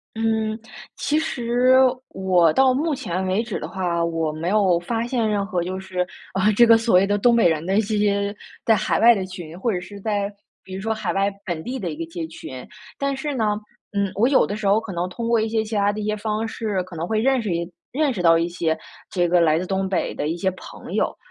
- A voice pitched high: Yes, high, 200 Hz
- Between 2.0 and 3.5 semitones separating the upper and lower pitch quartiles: No, average, 4.0 semitones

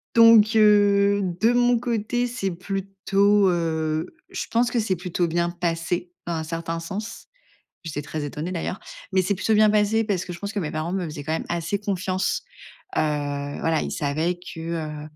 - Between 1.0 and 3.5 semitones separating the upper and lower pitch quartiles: No, average, 4.1 semitones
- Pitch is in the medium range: Yes, medium, 180 Hz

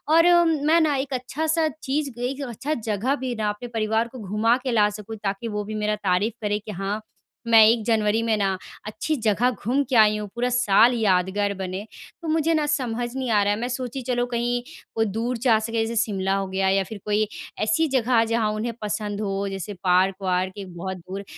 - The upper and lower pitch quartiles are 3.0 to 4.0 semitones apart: Yes, average, 3.4 semitones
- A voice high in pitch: Yes, high, 220 Hz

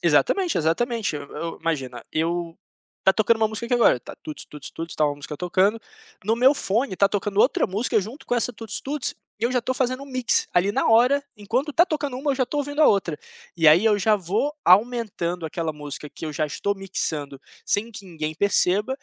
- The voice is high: Yes, high, 205 Hz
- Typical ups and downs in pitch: No, wide, 6.8 semitones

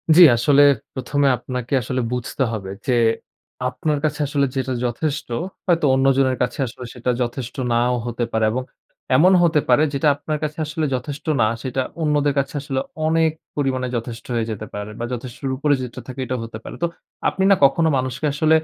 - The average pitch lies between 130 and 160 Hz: Yes, low, 135 Hz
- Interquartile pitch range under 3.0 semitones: No, average, 3.3 semitones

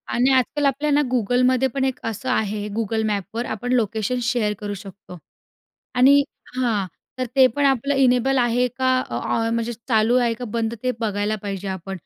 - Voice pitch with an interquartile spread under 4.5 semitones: Yes, average, 3.3 semitones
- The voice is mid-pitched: No, high, 235 Hz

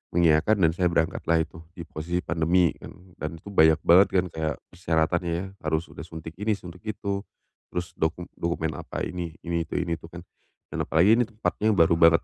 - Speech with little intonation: Yes, narrow, 1.9 semitones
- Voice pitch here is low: Yes, very low, 85 Hz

